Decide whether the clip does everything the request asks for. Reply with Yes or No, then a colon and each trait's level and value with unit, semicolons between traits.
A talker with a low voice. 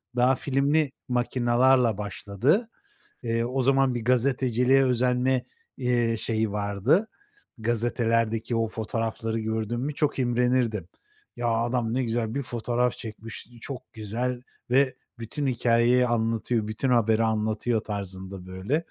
Yes: low, 120 Hz